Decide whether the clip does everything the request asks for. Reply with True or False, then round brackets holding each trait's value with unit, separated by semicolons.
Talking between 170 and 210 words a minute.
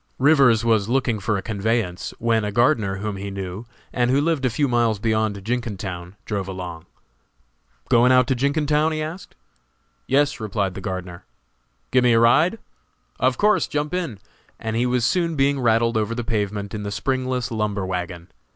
True (180 wpm)